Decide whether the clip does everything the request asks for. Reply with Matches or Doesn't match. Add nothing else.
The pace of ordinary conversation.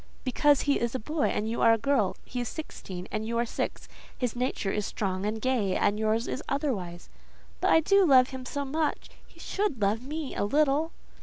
Doesn't match